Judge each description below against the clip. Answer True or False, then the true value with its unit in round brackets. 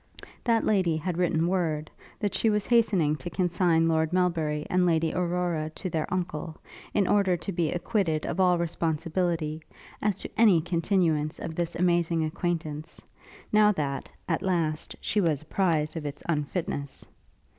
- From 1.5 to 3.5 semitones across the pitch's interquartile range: True (2.7 semitones)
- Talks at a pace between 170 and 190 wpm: False (155 wpm)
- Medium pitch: True (170 Hz)